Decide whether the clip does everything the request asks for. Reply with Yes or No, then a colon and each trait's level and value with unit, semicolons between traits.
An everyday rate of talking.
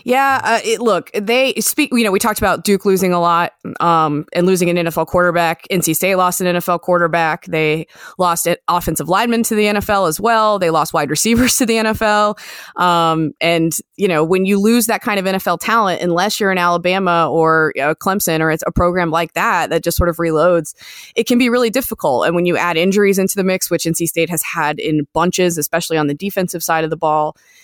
No: fast, 220 wpm